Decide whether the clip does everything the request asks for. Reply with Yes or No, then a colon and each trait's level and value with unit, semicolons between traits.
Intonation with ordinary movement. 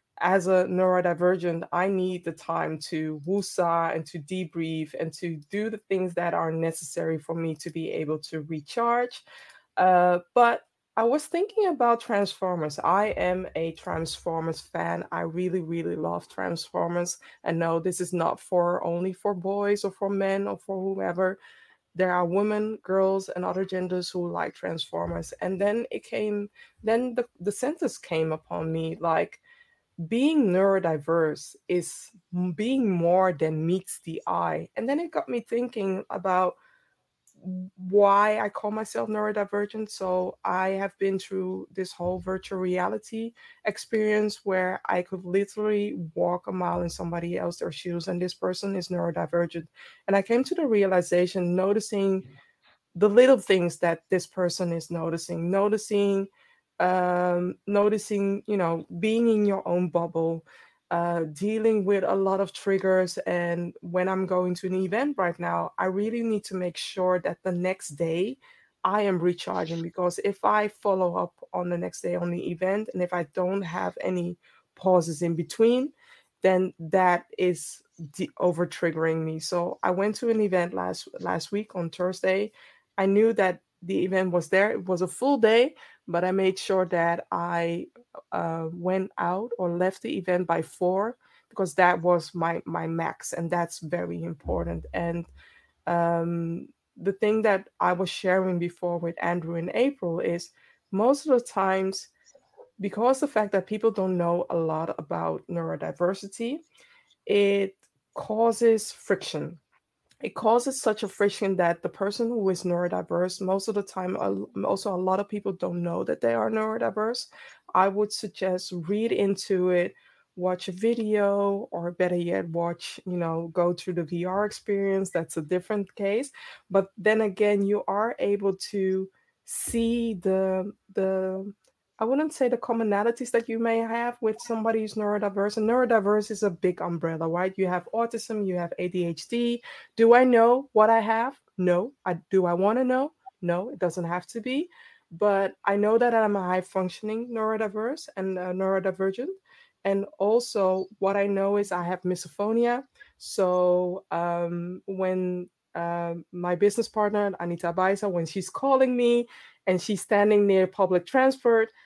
Yes: average, 3.4 semitones